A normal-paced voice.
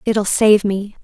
Yes: average, 175 wpm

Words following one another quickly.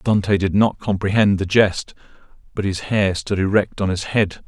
No: average, 190 wpm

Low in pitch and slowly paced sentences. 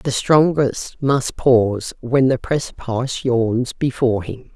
Yes: low, 125 Hz; slow, 130 wpm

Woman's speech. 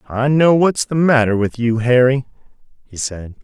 No: male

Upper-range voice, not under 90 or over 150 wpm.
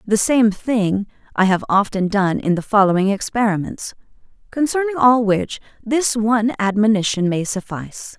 Yes: high, 215 Hz; average, 140 wpm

